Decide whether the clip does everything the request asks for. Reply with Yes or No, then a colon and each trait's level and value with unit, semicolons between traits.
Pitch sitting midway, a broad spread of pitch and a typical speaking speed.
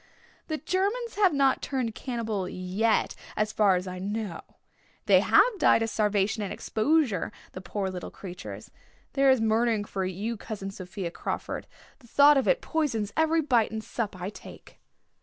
No: high, 220 Hz; wide, 5.9 semitones; average, 165 wpm